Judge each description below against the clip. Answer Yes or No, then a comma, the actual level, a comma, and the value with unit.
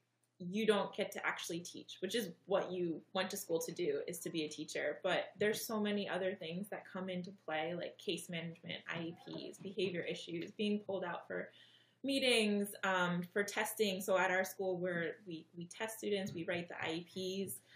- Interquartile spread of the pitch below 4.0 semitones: Yes, average, 2.9 semitones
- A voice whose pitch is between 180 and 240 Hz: Yes, medium, 185 Hz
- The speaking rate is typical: Yes, average, 195 wpm